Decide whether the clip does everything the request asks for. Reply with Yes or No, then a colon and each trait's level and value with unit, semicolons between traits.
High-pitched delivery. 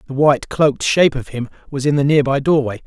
No: medium, 140 Hz